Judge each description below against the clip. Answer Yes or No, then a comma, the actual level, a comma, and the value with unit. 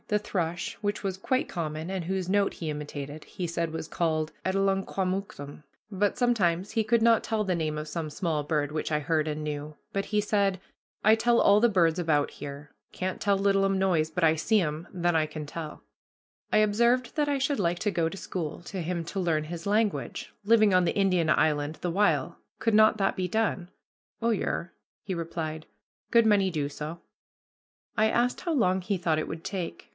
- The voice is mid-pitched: Yes, medium, 180 Hz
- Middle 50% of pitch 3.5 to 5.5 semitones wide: Yes, average, 4.4 semitones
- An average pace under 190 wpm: No, average, 200 wpm